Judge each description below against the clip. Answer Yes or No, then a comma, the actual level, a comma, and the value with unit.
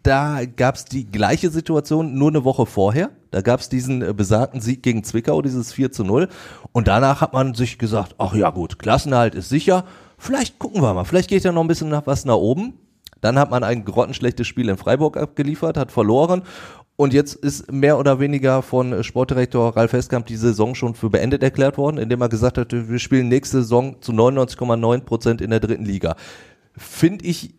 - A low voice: Yes, low, 125 Hz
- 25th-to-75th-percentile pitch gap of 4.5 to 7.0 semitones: No, average, 3.5 semitones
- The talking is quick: Yes, fast, 205 wpm